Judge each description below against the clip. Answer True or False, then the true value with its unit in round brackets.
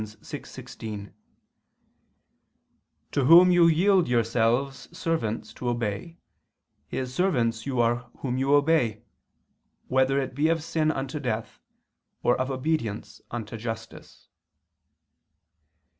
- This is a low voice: True (130 Hz)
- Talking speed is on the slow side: True (105 wpm)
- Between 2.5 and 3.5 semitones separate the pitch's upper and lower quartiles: False (5.2 semitones)